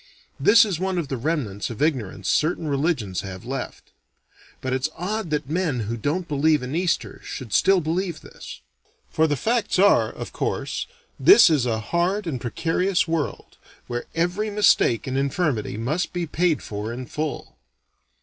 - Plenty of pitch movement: Yes, wide, 5.8 semitones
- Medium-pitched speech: Yes, medium, 155 Hz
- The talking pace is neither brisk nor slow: Yes, average, 165 wpm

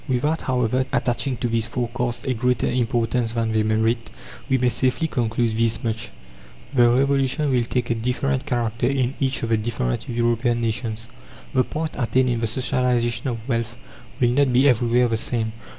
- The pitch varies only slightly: Yes, narrow, 2.0 semitones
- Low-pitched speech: Yes, low, 120 Hz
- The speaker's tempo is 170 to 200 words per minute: Yes, average, 175 wpm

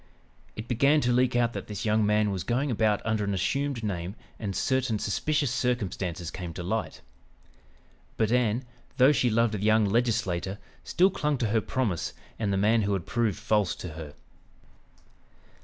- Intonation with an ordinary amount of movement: Yes, average, 3.6 semitones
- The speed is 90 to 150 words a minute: No, average, 175 wpm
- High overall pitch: No, low, 110 Hz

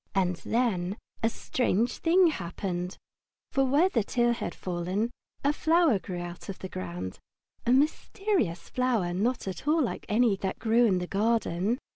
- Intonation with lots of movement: Yes, wide, 5.8 semitones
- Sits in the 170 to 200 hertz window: No, high, 220 Hz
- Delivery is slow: No, average, 160 wpm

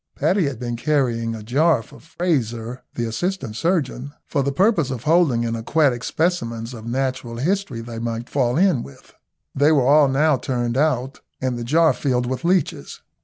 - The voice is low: Yes, low, 130 Hz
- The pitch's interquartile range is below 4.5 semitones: No, average, 4.9 semitones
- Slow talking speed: No, average, 175 wpm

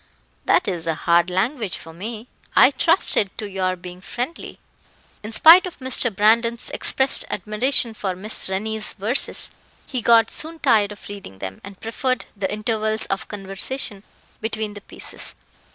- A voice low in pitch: No, high, 215 Hz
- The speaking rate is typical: Yes, average, 150 wpm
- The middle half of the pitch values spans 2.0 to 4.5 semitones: Yes, average, 3.5 semitones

